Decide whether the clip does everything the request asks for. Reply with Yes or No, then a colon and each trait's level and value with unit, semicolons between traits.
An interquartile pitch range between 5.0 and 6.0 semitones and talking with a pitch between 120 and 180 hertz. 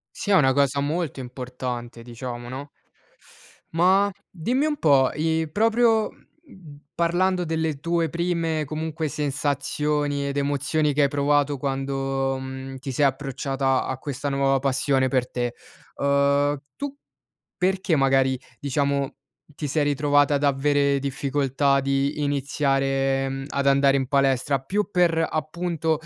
No: average, 2.7 semitones; medium, 140 Hz